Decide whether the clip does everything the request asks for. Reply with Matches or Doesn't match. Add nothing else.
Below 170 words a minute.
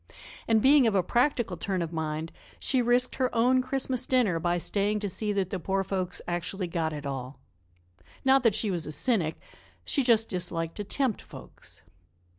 Doesn't match